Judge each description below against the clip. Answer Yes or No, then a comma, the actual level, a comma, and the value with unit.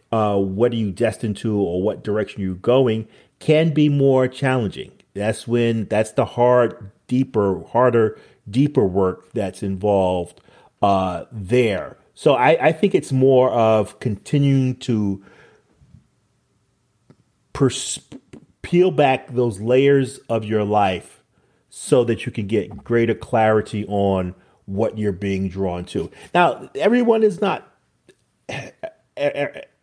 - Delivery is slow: Yes, slow, 125 wpm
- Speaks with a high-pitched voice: No, low, 115 Hz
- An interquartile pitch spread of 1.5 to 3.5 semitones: No, average, 4.3 semitones